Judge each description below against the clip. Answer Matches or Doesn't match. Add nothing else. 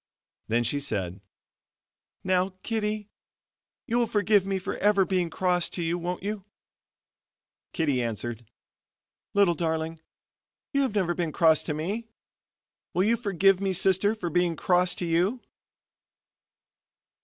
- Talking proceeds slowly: Matches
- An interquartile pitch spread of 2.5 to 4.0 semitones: Matches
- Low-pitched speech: Doesn't match